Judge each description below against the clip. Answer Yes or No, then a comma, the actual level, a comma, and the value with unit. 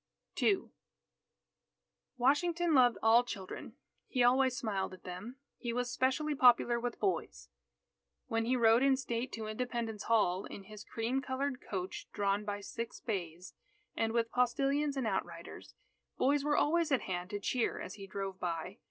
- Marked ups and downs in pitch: No, average, 4.6 semitones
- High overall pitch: Yes, high, 235 Hz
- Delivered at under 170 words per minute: Yes, average, 155 wpm